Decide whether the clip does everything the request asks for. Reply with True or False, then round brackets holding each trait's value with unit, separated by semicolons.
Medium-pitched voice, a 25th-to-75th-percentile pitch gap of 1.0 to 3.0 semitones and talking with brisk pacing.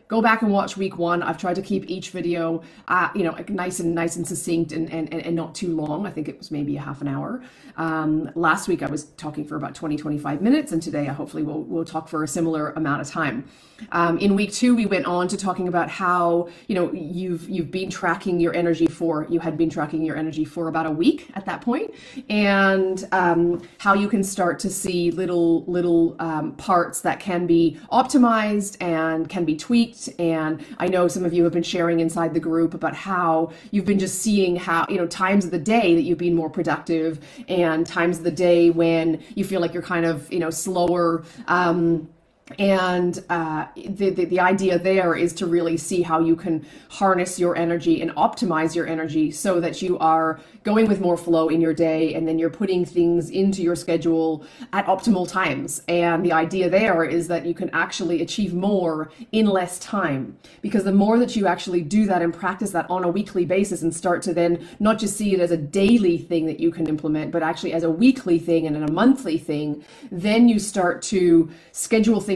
True (170 Hz; 2.6 semitones; 215 wpm)